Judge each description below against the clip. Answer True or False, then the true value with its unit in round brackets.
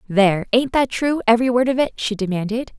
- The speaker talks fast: False (195 wpm)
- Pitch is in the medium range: False (230 Hz)